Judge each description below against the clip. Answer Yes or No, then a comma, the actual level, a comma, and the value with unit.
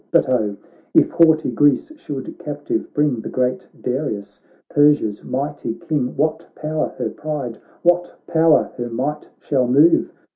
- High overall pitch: No, medium, 145 Hz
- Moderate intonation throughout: Yes, average, 3.6 semitones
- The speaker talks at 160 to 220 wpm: No, average, 140 wpm